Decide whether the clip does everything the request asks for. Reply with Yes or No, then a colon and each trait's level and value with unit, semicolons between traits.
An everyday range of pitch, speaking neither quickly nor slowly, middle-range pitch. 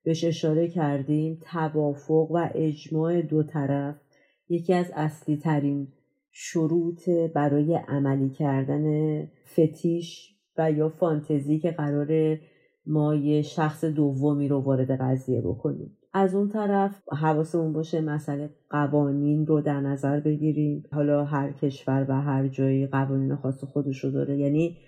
No: narrow, 2.2 semitones; average, 130 wpm; medium, 150 Hz